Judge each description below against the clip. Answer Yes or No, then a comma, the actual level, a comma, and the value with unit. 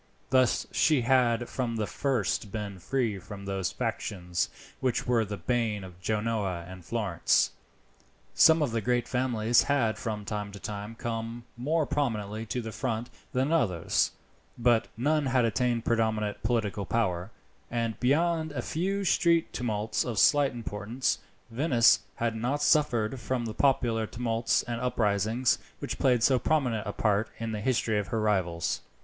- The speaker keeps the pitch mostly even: No, average, 3.3 semitones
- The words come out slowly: No, average, 155 wpm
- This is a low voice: Yes, low, 115 Hz